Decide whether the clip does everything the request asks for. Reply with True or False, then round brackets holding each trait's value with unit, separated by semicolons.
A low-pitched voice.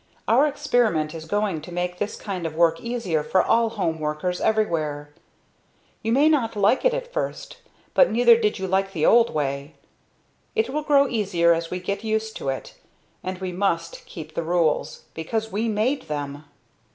False (190 Hz)